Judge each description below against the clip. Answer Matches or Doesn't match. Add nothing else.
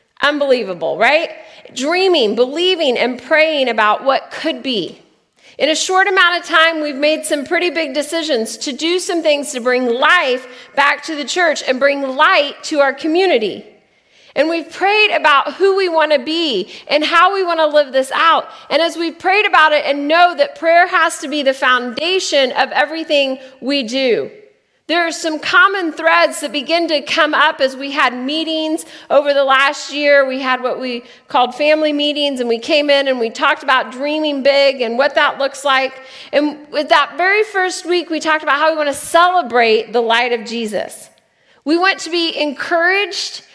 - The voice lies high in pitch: Matches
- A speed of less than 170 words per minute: Doesn't match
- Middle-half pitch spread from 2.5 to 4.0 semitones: Matches